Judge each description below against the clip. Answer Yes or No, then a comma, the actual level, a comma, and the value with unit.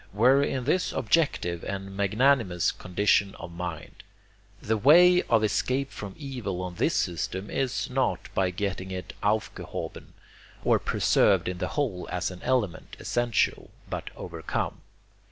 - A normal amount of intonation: No, wide, 5.9 semitones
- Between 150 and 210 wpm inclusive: No, slow, 135 wpm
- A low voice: Yes, low, 105 Hz